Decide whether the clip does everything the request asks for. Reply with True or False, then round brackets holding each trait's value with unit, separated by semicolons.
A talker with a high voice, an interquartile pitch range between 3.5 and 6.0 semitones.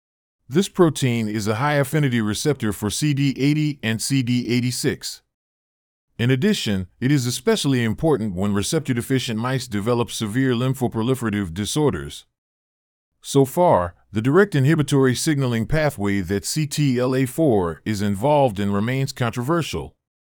False (125 Hz; 5.5 semitones)